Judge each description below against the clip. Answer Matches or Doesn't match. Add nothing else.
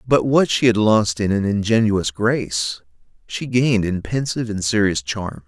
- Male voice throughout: Matches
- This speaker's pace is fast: Doesn't match